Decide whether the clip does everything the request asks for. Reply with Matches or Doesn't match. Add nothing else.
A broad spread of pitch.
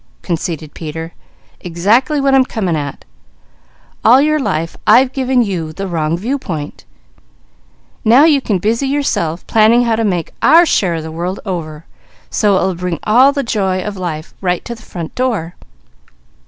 Matches